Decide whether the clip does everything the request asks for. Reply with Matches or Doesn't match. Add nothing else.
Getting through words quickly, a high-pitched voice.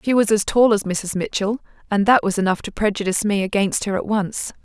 Matches